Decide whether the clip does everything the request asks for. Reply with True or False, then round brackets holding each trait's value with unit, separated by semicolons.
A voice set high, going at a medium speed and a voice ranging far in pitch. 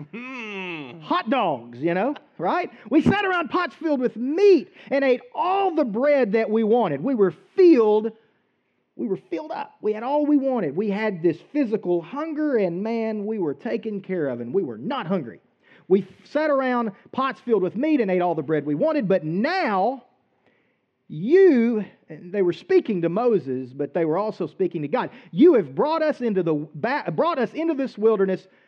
True (225 Hz; 190 wpm; 7.2 semitones)